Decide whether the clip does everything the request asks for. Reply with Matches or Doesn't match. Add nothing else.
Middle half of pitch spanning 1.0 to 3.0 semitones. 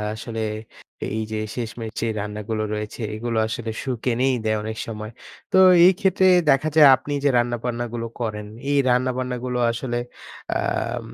Matches